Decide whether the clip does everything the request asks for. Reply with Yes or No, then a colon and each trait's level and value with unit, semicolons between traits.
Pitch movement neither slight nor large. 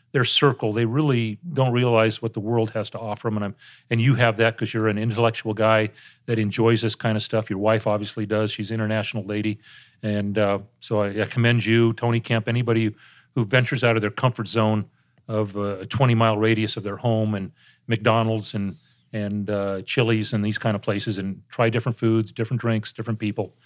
No: narrow, 1.5 semitones